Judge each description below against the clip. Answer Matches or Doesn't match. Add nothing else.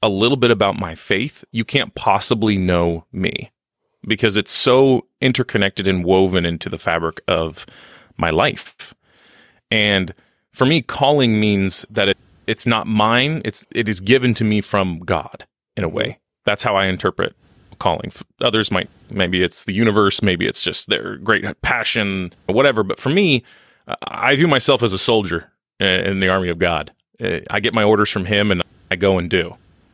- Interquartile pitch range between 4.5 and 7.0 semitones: Doesn't match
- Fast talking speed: Doesn't match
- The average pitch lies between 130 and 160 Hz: Doesn't match